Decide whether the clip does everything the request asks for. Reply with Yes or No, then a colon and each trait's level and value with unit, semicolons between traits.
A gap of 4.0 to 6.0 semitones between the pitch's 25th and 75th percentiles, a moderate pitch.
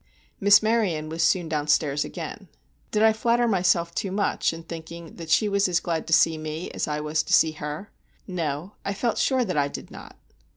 Yes: average, 4.5 semitones; medium, 170 Hz